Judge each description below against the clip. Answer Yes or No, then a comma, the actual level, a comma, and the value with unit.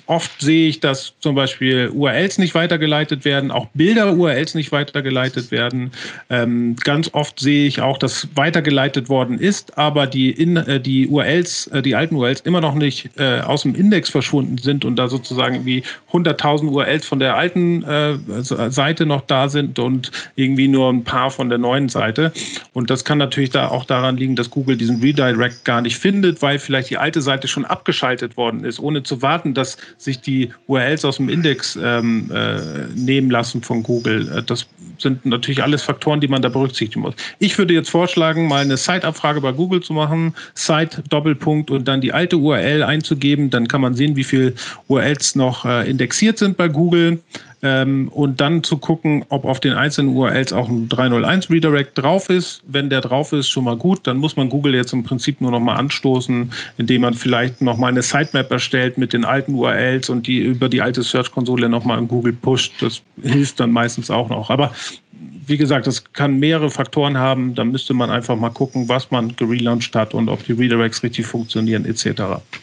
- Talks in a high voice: No, low, 135 Hz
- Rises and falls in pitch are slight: No, average, 3.0 semitones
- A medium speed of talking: No, fast, 195 wpm